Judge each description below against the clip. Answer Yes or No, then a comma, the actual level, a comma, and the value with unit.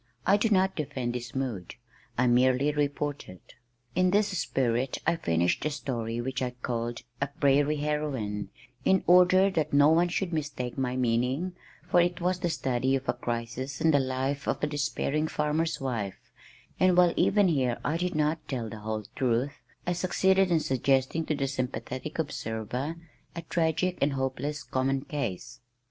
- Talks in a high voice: No, medium, 140 Hz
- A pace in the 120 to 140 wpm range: No, average, 170 wpm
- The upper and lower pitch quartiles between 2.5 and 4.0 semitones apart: No, average, 4.5 semitones